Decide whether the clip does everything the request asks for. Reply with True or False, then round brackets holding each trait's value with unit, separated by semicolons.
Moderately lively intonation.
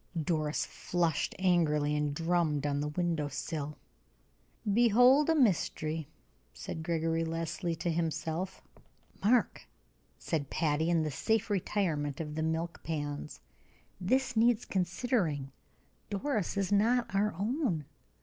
True (5.0 semitones)